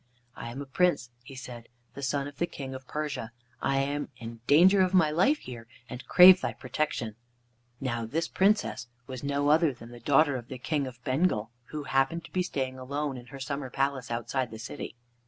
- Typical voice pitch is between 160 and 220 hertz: No, low, 135 Hz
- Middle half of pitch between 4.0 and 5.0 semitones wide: No, average, 3.5 semitones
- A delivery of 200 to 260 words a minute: Yes, fast, 205 wpm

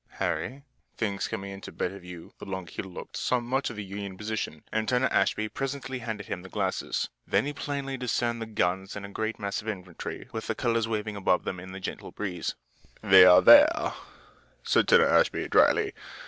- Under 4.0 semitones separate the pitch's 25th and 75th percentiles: No, average, 4.5 semitones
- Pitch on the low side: Yes, low, 105 Hz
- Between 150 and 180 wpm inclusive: No, average, 190 wpm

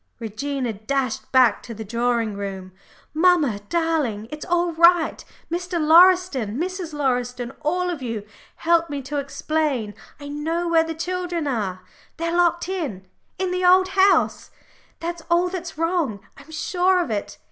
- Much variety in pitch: Yes, wide, 6.2 semitones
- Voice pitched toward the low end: No, very high, 315 Hz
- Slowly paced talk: No, average, 150 wpm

